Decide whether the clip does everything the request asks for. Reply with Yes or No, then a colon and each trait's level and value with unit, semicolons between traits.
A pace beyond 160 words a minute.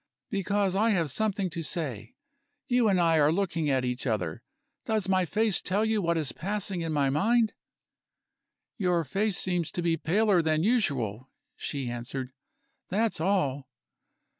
No: average, 155 wpm